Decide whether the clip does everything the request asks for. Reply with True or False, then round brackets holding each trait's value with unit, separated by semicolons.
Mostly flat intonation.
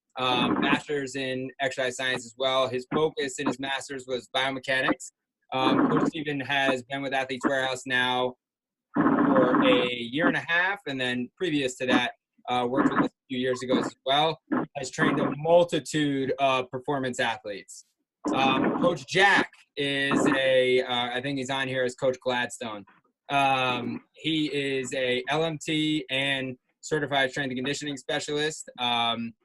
True (1.9 semitones)